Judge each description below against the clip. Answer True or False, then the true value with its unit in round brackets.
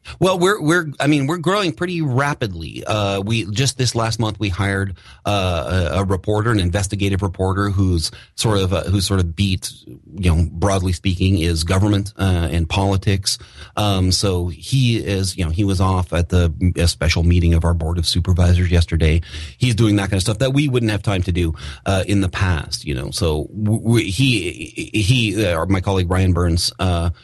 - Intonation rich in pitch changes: False (3.6 semitones)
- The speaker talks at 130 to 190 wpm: False (200 wpm)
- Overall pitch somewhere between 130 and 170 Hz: False (95 Hz)